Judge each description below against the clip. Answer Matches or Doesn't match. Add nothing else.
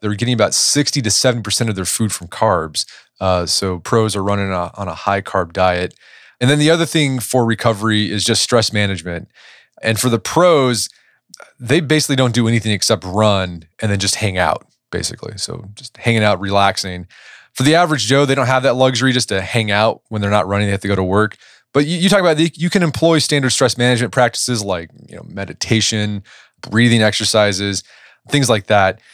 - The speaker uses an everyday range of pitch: Matches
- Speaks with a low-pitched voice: Matches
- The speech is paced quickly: Matches